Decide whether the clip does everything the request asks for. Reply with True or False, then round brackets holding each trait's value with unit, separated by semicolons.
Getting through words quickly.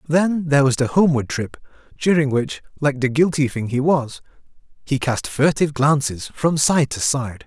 False (175 wpm)